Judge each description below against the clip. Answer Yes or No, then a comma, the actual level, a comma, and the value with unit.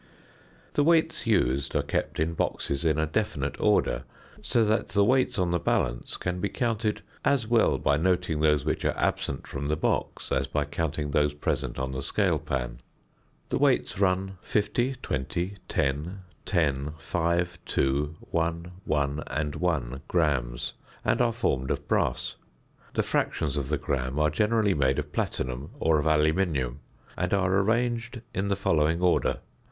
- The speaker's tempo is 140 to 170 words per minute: Yes, average, 165 wpm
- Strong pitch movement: Yes, wide, 5.9 semitones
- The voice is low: Yes, very low, 80 Hz